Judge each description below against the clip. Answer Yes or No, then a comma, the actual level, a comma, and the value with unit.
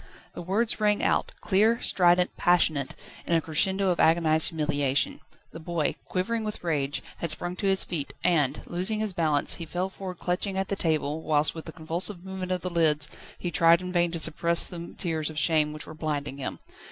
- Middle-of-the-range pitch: Yes, medium, 170 Hz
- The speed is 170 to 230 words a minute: Yes, average, 200 wpm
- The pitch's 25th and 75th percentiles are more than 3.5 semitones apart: No, average, 2.9 semitones